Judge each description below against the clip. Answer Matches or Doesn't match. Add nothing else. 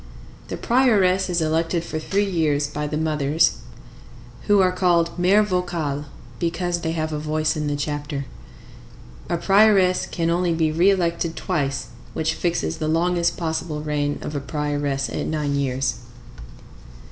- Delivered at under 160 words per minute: Matches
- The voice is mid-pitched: Matches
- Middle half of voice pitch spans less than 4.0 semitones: Matches